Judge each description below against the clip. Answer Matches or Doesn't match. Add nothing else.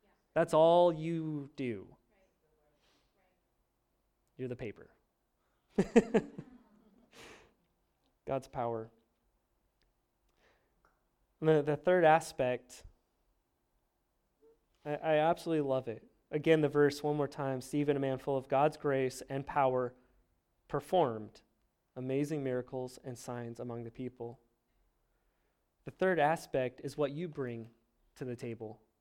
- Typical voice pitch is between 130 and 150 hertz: Matches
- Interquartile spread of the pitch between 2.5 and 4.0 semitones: Doesn't match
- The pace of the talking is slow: Matches